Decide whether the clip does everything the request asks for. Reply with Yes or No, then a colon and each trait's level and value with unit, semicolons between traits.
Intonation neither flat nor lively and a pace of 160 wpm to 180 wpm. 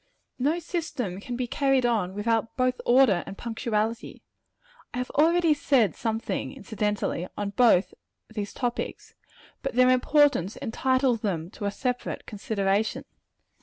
No: average, 4.0 semitones; slow, 135 wpm